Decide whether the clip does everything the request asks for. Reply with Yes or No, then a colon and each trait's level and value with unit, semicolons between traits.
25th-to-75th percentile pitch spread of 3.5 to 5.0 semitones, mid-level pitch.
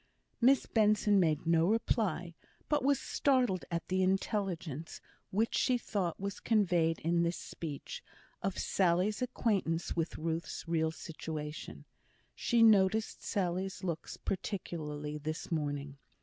Yes: average, 4.4 semitones; medium, 180 Hz